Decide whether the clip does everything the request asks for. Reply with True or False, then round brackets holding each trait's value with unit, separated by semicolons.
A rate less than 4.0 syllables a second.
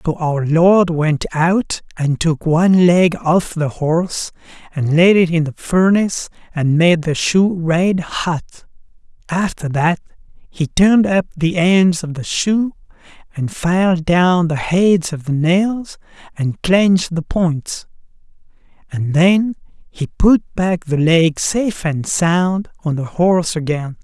True (3.7 syllables/s)